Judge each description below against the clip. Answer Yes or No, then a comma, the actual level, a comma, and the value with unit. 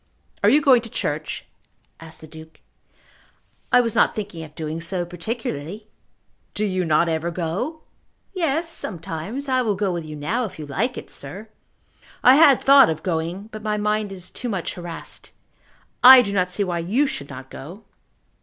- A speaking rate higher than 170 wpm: Yes, average, 180 wpm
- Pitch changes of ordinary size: No, wide, 6.2 semitones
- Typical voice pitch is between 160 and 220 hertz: Yes, high, 190 Hz